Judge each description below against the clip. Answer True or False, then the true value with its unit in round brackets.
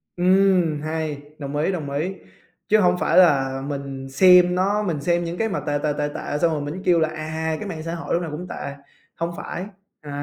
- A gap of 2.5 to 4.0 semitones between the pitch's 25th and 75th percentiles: True (3.6 semitones)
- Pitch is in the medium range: True (160 Hz)